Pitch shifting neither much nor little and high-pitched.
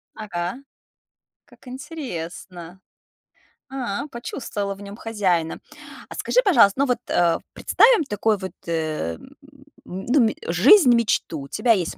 No: wide, 6.2 semitones; high, 205 Hz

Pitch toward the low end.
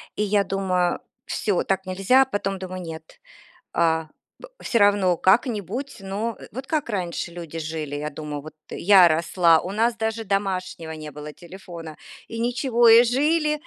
No: high, 190 Hz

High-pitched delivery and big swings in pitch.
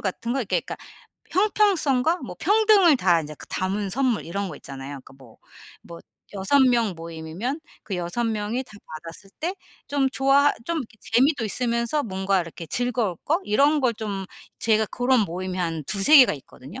Yes: high, 225 Hz; wide, 6.6 semitones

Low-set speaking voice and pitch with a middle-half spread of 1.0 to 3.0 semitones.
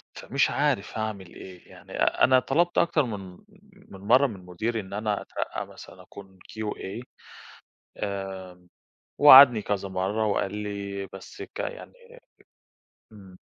No: low, 105 Hz; average, 3.7 semitones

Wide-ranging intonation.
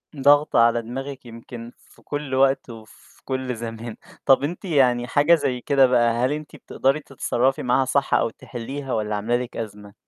No: average, 2.8 semitones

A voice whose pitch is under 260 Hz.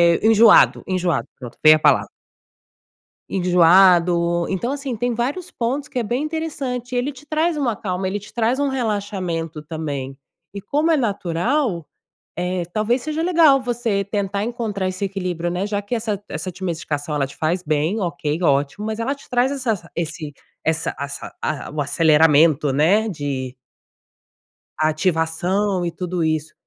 Yes: high, 190 Hz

